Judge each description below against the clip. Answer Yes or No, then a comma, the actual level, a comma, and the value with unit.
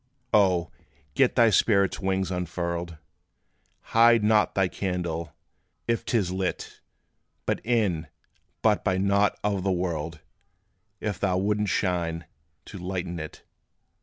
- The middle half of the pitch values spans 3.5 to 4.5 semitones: No, average, 3.1 semitones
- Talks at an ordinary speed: No, slow, 125 wpm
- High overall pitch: No, very low, 95 Hz